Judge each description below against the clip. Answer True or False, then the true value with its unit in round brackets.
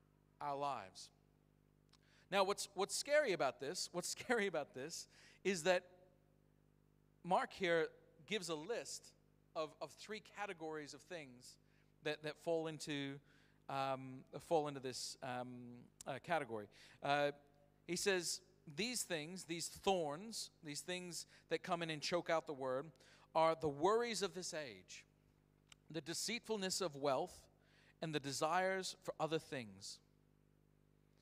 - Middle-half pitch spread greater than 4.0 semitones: True (4.4 semitones)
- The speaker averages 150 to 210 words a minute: False (135 wpm)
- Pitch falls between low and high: True (160 Hz)